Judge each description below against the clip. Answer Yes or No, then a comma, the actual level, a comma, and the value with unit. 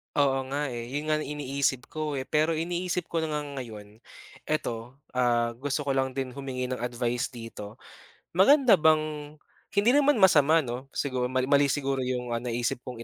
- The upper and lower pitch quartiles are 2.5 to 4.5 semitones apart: Yes, average, 3.7 semitones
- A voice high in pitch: No, low, 135 Hz